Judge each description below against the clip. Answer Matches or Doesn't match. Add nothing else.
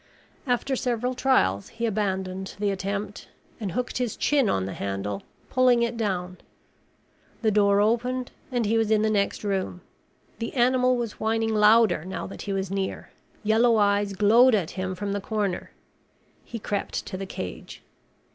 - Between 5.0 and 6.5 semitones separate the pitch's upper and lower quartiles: Doesn't match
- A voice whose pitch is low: Doesn't match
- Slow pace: Doesn't match